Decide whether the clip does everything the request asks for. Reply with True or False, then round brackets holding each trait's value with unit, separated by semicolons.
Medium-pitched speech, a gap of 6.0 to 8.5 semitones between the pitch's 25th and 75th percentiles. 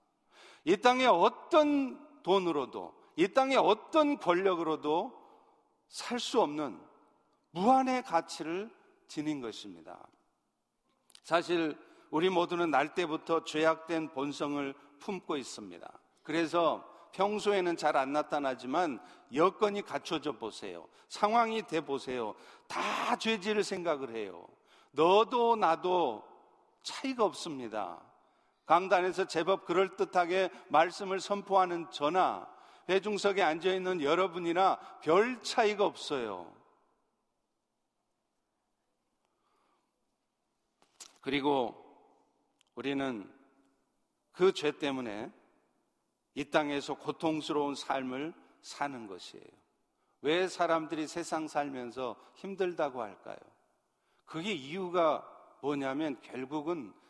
True (180 Hz; 6.3 semitones)